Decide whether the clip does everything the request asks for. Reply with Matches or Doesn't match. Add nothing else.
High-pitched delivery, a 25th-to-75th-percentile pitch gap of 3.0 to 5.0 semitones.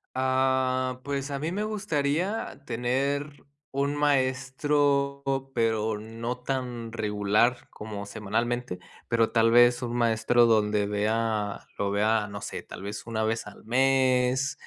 Doesn't match